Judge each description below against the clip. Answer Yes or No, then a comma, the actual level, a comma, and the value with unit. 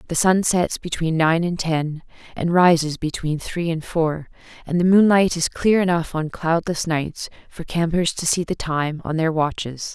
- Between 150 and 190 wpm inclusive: Yes, average, 185 wpm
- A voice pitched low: No, medium, 165 Hz